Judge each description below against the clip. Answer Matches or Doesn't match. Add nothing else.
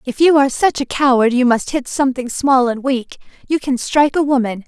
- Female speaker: Matches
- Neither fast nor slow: Doesn't match